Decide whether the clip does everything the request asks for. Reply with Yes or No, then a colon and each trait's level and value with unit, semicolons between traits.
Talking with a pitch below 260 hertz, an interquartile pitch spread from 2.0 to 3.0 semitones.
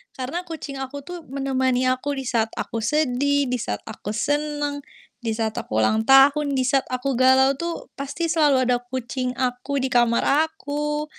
No: very high, 270 Hz; average, 2.7 semitones